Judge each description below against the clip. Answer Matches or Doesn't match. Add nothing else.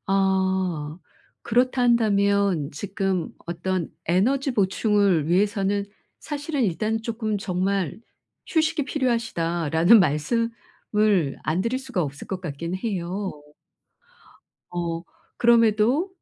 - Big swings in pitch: Doesn't match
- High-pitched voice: Matches